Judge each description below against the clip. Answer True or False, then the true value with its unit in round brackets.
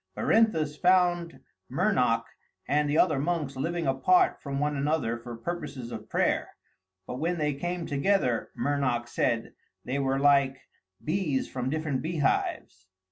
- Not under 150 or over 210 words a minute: False (135 wpm)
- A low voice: False (145 Hz)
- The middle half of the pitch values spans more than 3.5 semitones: True (4.1 semitones)